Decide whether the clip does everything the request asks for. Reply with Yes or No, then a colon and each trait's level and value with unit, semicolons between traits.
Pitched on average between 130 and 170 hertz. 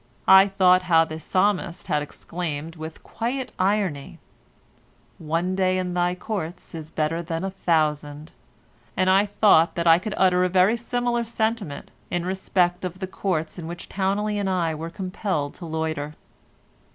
No: medium, 180 Hz